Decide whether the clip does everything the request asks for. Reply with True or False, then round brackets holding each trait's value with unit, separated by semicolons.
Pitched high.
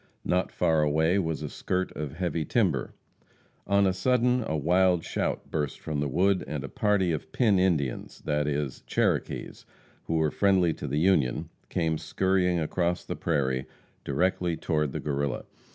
False (80 Hz)